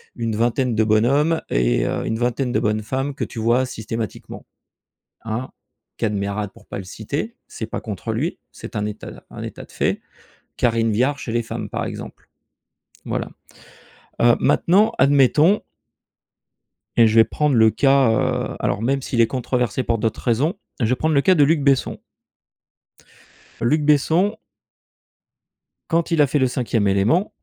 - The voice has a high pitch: No, low, 120 Hz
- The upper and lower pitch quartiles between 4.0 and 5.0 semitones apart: Yes, average, 4.3 semitones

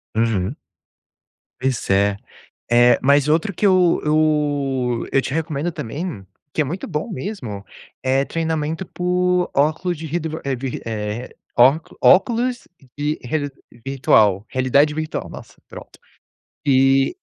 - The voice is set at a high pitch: No, medium, 145 Hz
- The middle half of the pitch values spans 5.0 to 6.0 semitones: No, average, 4.2 semitones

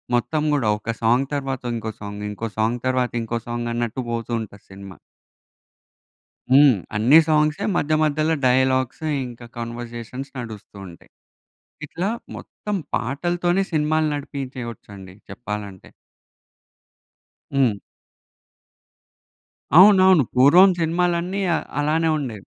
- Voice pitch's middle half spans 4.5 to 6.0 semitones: Yes, average, 5.1 semitones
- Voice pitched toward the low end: Yes, low, 130 Hz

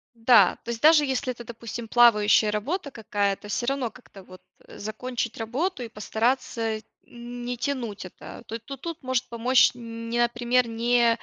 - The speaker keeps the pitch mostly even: Yes, narrow, 2.1 semitones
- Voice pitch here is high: Yes, high, 235 Hz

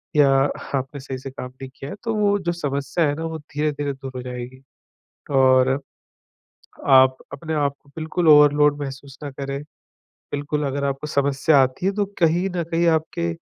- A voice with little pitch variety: No, average, 3.0 semitones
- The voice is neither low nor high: Yes, medium, 145 Hz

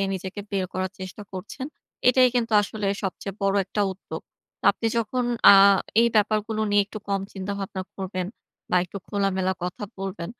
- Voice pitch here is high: Yes, high, 195 Hz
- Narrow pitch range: Yes, narrow, 2.2 semitones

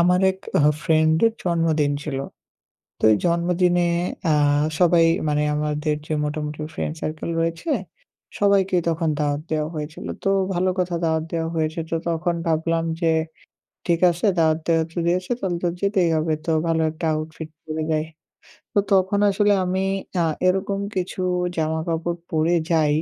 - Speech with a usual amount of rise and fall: No, narrow, 2.2 semitones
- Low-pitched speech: No, medium, 165 Hz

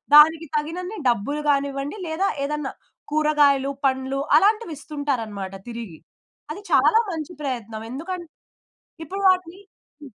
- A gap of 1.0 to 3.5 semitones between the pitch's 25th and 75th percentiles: No, average, 3.9 semitones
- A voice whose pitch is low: No, very high, 295 Hz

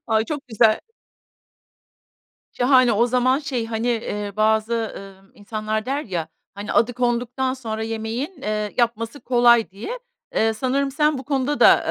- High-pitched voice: Yes, high, 235 Hz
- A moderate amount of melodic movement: Yes, average, 3.0 semitones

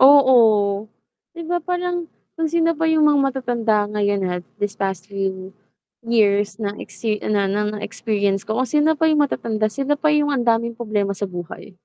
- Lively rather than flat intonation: Yes, wide, 6.3 semitones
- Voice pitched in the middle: No, high, 225 Hz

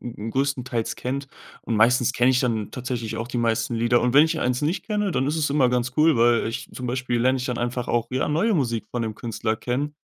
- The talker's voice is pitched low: Yes, low, 125 Hz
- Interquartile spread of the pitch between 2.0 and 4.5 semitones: Yes, narrow, 2.6 semitones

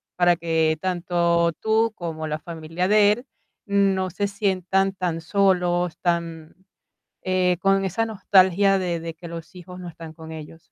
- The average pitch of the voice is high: No, medium, 180 Hz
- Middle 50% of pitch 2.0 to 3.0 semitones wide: Yes, narrow, 2.6 semitones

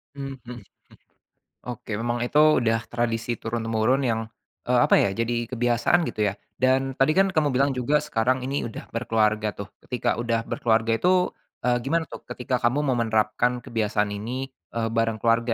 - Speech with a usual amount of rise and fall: No, narrow, 2.3 semitones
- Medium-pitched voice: No, low, 120 Hz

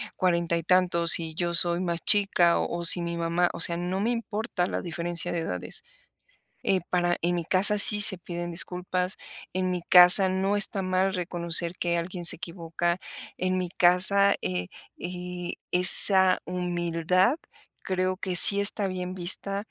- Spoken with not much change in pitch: Yes, narrow, 1.5 semitones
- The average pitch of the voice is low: No, medium, 180 Hz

